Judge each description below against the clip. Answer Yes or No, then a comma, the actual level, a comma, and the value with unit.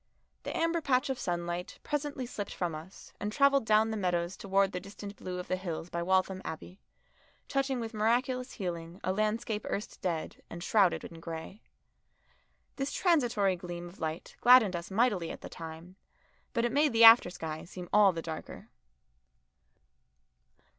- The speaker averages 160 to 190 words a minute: Yes, average, 165 wpm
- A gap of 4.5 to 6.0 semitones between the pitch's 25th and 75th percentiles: Yes, average, 5.2 semitones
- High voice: Yes, high, 195 Hz